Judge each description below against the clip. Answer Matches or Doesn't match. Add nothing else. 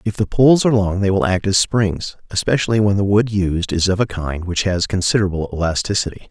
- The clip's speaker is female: Doesn't match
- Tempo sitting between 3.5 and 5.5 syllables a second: Doesn't match